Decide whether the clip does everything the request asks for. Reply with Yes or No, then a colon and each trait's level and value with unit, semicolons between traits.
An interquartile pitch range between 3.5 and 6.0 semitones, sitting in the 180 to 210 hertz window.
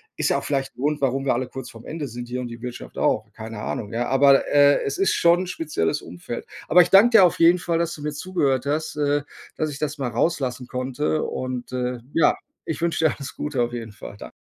No: average, 4.2 semitones; medium, 140 Hz